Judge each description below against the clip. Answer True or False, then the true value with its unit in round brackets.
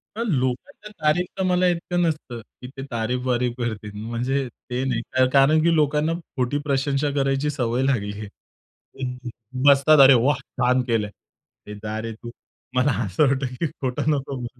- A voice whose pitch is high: False (130 Hz)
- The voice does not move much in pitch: False (3.4 semitones)